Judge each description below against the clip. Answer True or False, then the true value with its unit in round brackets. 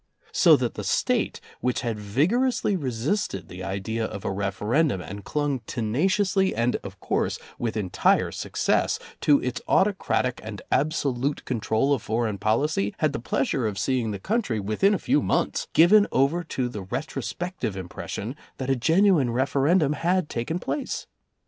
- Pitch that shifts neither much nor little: False (7.0 semitones)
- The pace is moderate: True (155 wpm)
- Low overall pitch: True (130 Hz)